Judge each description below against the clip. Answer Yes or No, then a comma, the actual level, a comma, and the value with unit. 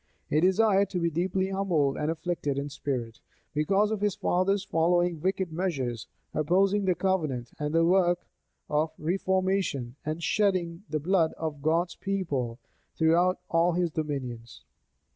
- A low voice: No, medium, 170 Hz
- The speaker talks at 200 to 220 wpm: No, average, 145 wpm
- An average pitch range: Yes, average, 4.0 semitones